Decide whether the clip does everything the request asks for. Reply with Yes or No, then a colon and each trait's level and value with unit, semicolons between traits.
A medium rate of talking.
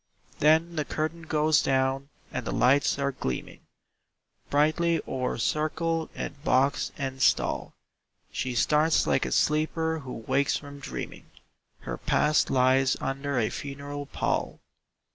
No: slow, 130 wpm